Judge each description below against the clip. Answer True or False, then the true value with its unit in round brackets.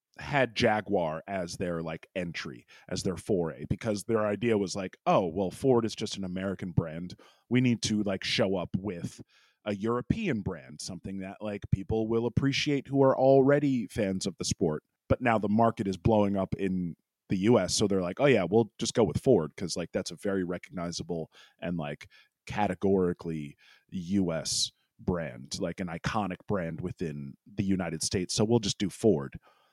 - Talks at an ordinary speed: True (180 wpm)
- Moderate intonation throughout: True (3.8 semitones)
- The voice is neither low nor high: False (100 Hz)